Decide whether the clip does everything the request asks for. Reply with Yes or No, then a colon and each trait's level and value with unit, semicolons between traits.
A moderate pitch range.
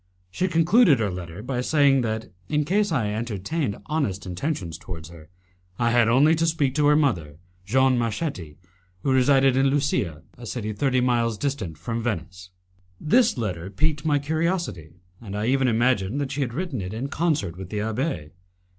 No: wide, 6.6 semitones